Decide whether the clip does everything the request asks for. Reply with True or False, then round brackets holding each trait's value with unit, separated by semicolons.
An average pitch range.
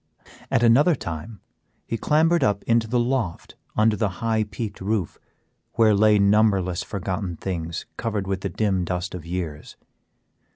True (3.7 semitones)